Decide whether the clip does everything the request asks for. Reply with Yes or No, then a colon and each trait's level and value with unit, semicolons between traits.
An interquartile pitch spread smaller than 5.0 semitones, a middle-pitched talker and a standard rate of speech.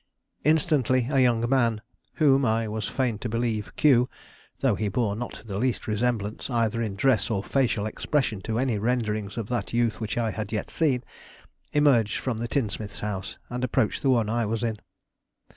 No: average, 2.8 semitones; low, 115 Hz; average, 180 wpm